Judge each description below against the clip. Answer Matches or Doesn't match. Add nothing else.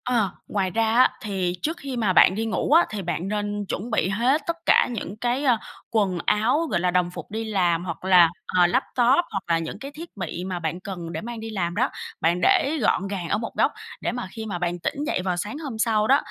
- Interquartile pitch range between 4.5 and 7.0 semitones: Matches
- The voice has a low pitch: Doesn't match